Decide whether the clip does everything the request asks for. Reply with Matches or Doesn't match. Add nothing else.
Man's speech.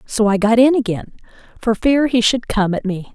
Doesn't match